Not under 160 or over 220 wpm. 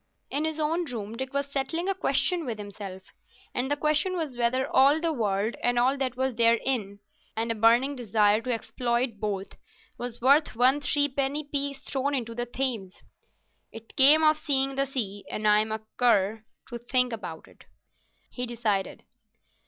Yes: average, 170 wpm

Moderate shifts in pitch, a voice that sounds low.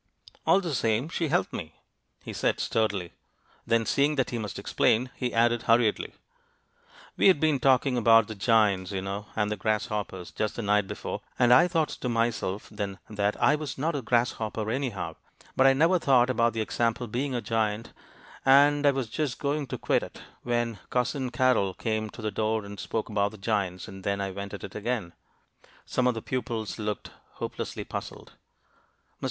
Yes: average, 3.6 semitones; low, 115 Hz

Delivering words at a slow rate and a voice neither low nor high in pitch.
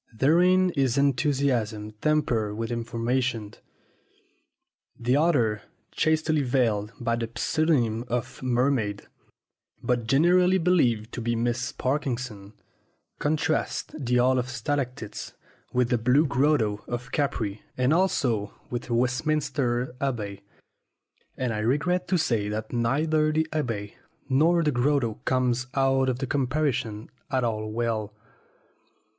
No: slow, 120 wpm; low, 125 Hz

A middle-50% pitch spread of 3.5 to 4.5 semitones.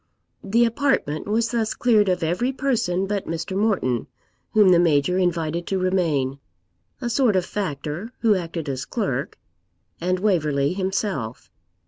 No: average, 4.9 semitones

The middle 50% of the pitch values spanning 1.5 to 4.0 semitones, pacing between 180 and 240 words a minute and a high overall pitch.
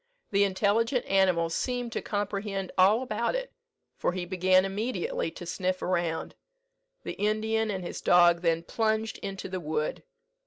No: average, 3.4 semitones; average, 150 wpm; high, 195 Hz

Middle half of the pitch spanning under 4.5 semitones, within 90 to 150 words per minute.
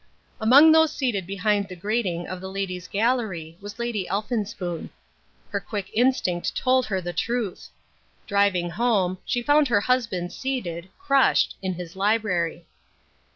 No: average, 4.9 semitones; average, 140 wpm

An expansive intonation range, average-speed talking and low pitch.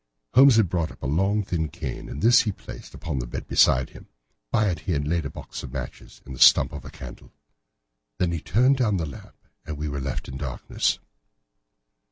No: wide, 5.9 semitones; fast, 215 wpm; very low, 80 Hz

